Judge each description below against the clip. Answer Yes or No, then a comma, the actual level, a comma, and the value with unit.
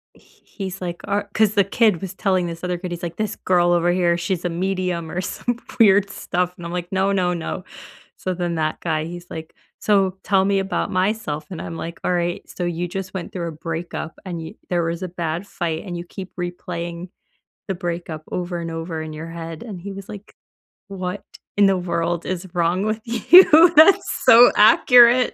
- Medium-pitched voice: Yes, medium, 180 Hz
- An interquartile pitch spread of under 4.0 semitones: Yes, narrow, 2.4 semitones